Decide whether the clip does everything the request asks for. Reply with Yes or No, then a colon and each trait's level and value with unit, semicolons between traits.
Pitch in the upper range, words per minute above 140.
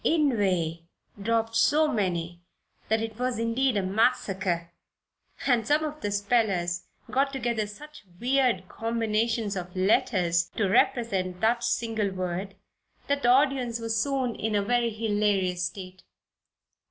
No: high, 220 Hz; slow, 135 wpm